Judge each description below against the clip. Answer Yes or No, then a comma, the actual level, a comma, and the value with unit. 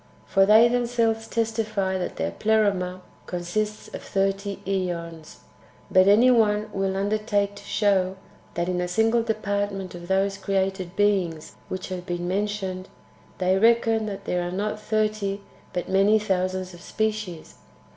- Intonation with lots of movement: No, narrow, 2.6 semitones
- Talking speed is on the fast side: No, average, 145 wpm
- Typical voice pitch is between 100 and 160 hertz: No, high, 195 Hz